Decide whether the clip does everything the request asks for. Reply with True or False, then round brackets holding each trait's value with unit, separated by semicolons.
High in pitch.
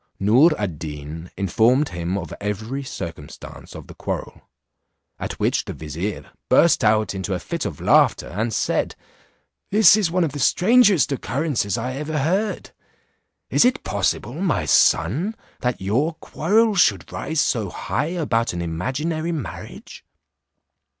False (130 Hz)